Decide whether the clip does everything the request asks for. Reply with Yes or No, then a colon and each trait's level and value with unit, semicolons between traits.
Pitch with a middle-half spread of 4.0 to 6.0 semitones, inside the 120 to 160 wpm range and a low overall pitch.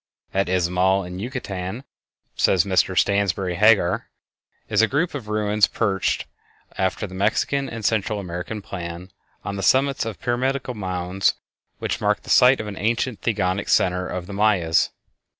No: average, 3.5 semitones; average, 150 wpm; low, 100 Hz